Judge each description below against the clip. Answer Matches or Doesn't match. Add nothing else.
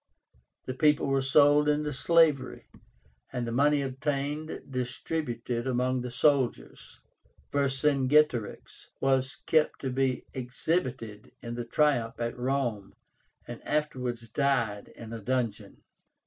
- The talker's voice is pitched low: Matches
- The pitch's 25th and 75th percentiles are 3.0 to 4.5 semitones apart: Matches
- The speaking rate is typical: Doesn't match